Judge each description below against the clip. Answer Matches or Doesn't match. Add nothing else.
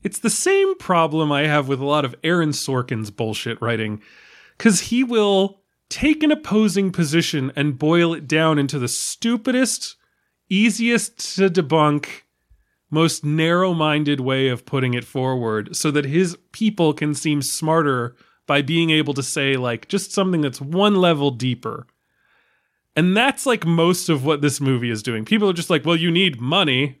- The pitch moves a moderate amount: Doesn't match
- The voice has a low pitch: Doesn't match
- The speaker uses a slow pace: Doesn't match